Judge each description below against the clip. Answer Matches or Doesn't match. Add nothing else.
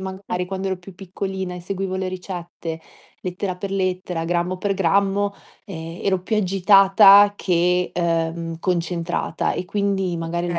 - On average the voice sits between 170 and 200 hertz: Matches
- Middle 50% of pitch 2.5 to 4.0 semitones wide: Doesn't match